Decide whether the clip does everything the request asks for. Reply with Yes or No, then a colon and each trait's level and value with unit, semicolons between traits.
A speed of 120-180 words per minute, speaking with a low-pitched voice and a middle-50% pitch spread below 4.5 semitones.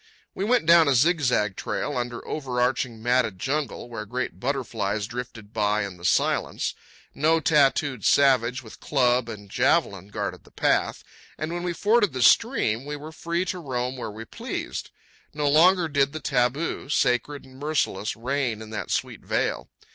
No: average, 165 wpm; low, 130 Hz; average, 5.0 semitones